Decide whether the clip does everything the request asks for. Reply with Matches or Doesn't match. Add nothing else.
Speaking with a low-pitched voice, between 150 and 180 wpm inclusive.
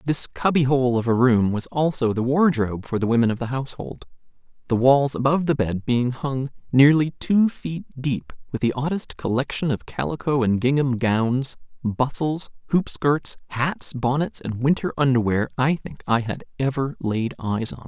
Matches